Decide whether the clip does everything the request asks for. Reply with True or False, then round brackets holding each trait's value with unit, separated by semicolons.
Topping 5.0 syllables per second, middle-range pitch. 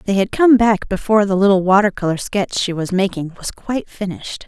False (5.8 syllables/s; 200 Hz)